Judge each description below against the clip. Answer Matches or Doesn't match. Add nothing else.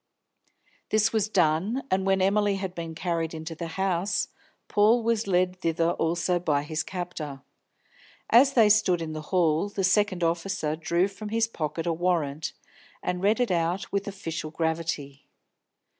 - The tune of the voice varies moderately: Matches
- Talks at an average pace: Matches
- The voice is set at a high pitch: Doesn't match